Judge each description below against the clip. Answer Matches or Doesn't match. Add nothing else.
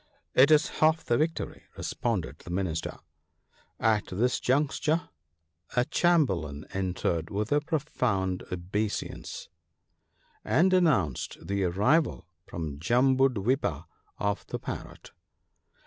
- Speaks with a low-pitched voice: Matches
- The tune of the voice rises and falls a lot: Matches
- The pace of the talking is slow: Matches